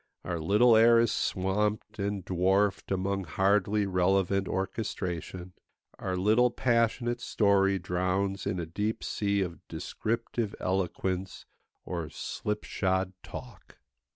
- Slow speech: Yes, slow, 110 wpm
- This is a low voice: Yes, very low, 95 Hz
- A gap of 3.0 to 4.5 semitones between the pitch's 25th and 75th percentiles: No, narrow, 2.4 semitones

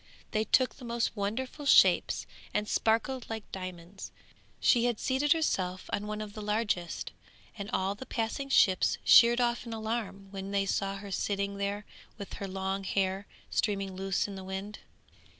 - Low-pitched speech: No, high, 205 Hz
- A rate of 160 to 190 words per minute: Yes, average, 170 wpm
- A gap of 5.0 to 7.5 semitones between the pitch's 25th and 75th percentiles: No, average, 2.9 semitones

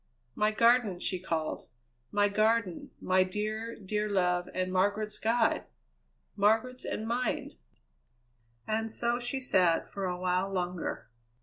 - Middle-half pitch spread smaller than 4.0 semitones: Yes, average, 3.4 semitones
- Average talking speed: No, slow, 125 wpm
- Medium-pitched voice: No, high, 205 Hz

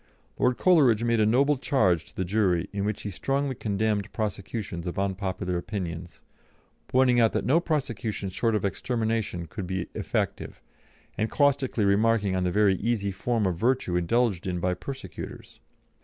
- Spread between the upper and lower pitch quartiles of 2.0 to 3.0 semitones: No, average, 4.4 semitones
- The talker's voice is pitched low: Yes, low, 105 Hz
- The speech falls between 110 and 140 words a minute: No, average, 160 wpm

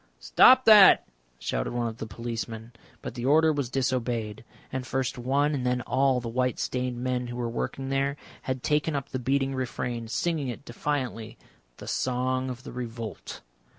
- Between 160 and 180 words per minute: Yes, average, 175 wpm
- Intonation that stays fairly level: Yes, narrow, 2.3 semitones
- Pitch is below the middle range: Yes, low, 125 Hz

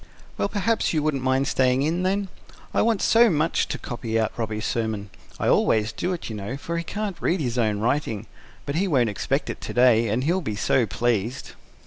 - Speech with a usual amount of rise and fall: No, wide, 7.1 semitones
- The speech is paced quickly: Yes, fast, 210 wpm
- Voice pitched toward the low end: Yes, low, 130 Hz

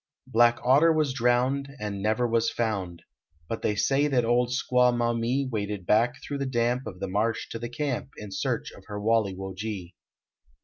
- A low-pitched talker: Yes, low, 120 Hz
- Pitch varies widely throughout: No, average, 3.3 semitones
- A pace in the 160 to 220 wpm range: Yes, average, 185 wpm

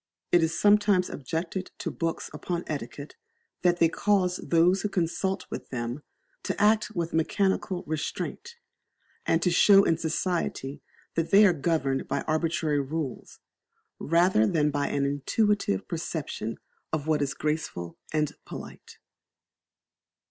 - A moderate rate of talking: No, slow, 130 wpm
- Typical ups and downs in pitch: Yes, average, 3.8 semitones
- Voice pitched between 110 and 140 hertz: No, medium, 165 Hz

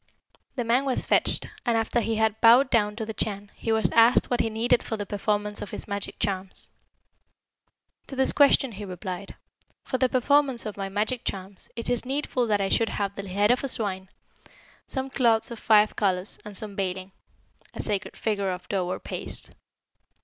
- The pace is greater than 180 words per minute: Yes, average, 195 wpm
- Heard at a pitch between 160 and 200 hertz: No, high, 215 Hz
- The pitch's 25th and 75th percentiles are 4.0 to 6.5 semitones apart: No, average, 3.3 semitones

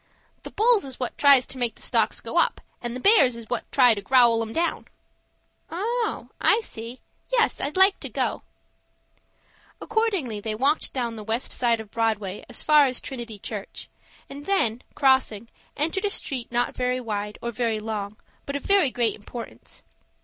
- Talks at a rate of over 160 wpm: Yes, average, 180 wpm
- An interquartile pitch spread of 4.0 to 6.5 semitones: Yes, average, 4.5 semitones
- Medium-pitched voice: No, high, 245 Hz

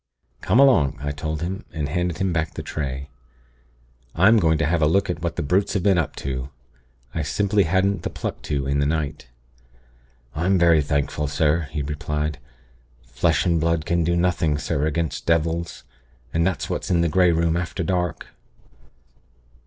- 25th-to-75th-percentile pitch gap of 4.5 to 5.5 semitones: No, average, 2.9 semitones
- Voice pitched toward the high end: No, very low, 80 Hz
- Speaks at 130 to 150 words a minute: No, average, 175 wpm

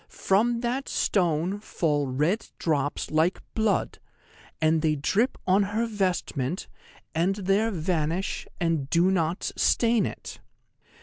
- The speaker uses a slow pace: Yes, slow, 120 wpm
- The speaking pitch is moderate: Yes, medium, 180 Hz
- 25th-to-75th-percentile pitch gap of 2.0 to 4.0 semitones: No, average, 4.7 semitones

